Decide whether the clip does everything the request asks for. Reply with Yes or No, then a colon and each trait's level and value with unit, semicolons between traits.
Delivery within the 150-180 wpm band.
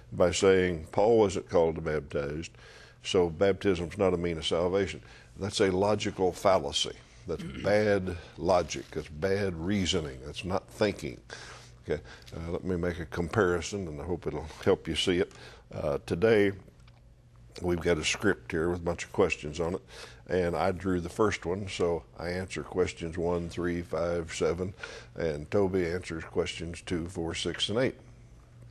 Yes: average, 165 wpm